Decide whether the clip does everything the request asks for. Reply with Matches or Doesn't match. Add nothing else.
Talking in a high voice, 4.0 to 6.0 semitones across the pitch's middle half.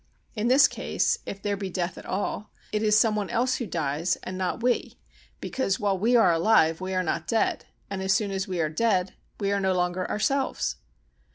Doesn't match